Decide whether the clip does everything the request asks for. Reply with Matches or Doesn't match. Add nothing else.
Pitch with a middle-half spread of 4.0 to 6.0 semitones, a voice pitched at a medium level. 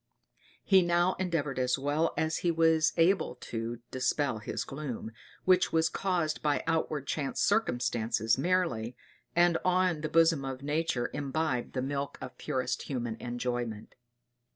Matches